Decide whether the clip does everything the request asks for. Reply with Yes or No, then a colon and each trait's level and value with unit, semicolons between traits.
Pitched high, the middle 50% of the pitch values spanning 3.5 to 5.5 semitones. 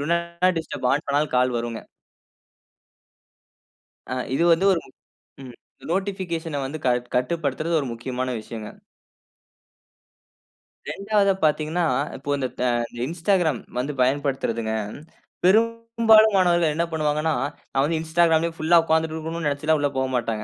No: medium, 155 Hz; average, 4.4 semitones